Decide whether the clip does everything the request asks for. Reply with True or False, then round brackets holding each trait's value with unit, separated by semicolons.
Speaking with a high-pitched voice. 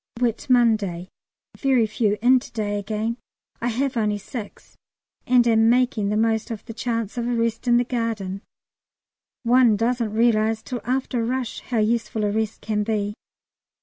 True (230 Hz)